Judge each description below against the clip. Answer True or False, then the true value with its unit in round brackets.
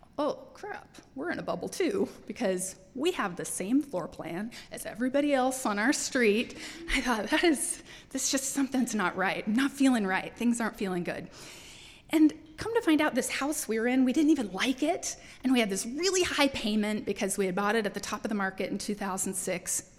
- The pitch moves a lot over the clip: True (5.8 semitones)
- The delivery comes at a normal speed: False (215 wpm)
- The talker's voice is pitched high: True (240 Hz)